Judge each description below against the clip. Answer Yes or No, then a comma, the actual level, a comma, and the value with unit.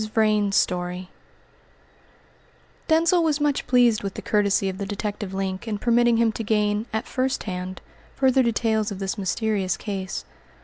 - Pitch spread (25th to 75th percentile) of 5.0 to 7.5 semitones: No, average, 3.4 semitones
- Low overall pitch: No, high, 210 Hz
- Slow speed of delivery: No, average, 150 wpm